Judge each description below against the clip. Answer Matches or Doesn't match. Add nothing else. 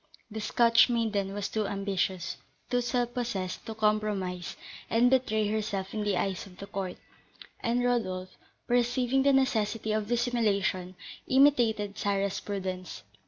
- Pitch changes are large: Doesn't match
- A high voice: Matches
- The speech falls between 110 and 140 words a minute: Matches